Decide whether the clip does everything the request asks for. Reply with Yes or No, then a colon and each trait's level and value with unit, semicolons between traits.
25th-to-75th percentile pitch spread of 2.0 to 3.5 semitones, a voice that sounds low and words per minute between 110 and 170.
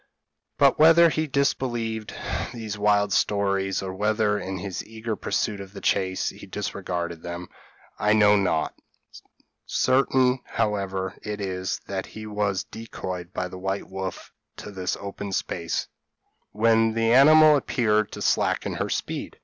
Yes: average, 2.9 semitones; low, 105 Hz; average, 140 wpm